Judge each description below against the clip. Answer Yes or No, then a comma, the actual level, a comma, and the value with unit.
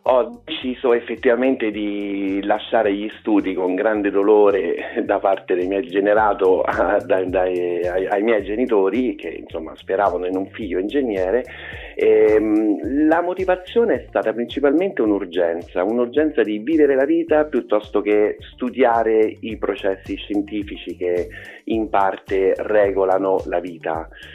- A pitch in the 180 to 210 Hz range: No, low, 110 Hz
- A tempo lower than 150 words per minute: Yes, average, 130 wpm